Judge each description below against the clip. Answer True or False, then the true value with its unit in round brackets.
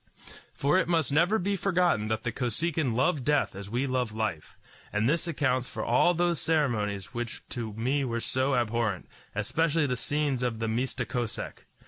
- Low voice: True (130 Hz)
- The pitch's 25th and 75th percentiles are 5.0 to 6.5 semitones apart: True (5.3 semitones)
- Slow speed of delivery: False (175 wpm)